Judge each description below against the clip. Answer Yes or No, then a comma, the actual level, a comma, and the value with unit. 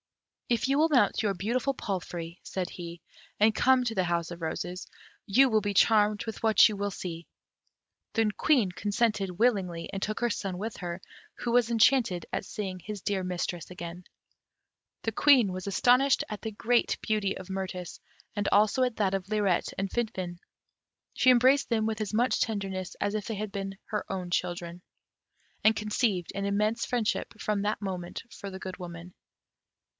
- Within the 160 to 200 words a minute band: Yes, average, 180 wpm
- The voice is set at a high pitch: Yes, high, 205 Hz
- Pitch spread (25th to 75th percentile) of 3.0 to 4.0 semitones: Yes, average, 3.5 semitones